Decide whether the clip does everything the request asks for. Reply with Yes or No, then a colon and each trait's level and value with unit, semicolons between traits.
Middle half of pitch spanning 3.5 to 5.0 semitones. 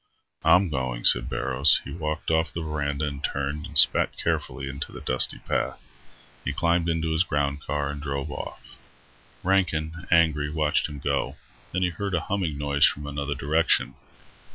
No: narrow, 2.6 semitones